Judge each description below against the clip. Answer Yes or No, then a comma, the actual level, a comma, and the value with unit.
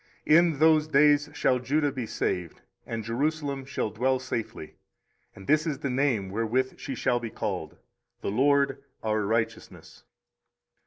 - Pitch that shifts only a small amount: No, average, 4.3 semitones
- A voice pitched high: No, low, 130 Hz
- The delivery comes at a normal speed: Yes, average, 150 wpm